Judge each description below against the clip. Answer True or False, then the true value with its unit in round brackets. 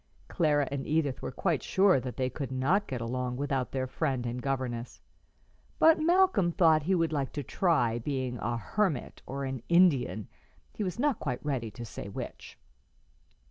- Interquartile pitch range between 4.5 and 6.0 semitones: True (5.3 semitones)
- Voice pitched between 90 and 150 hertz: True (135 Hz)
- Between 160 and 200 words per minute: True (175 wpm)